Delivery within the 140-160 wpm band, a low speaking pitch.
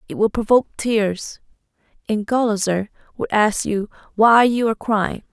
No: average, 145 wpm; high, 215 Hz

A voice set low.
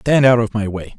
Yes: low, 115 Hz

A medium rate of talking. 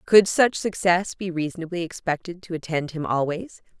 Yes: average, 160 wpm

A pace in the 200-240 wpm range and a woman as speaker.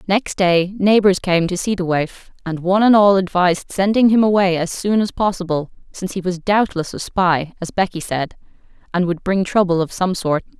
Yes: fast, 205 wpm; female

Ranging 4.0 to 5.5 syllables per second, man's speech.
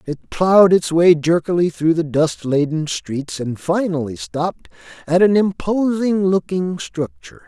Yes: 4.3 syllables/s; male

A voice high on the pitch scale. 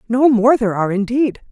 Yes: high, 230 Hz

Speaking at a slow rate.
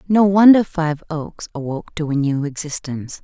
No: average, 165 wpm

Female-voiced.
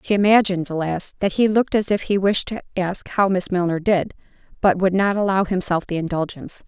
Yes: female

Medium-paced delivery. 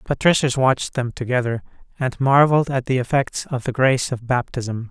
Yes: average, 170 wpm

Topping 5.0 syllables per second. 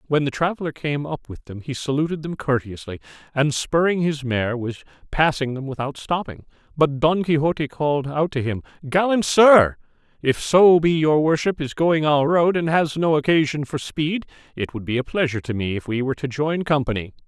Yes: 5.3 syllables/s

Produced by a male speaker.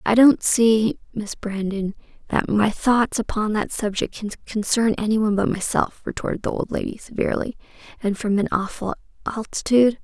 No: female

